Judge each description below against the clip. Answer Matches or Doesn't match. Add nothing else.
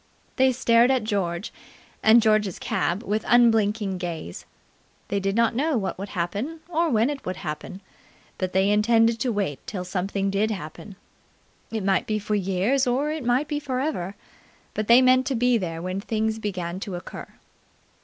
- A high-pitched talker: Matches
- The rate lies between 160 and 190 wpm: Matches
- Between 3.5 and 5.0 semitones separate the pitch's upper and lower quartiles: Matches